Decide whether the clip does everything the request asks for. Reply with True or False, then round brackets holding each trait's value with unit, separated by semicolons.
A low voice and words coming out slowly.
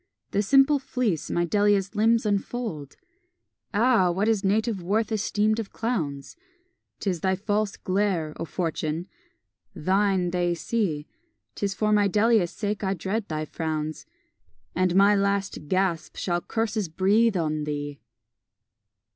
False (195 Hz; 130 wpm)